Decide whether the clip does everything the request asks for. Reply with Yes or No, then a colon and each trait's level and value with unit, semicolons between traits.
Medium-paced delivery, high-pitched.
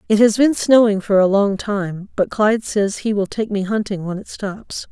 No: fast, 230 wpm; high, 205 Hz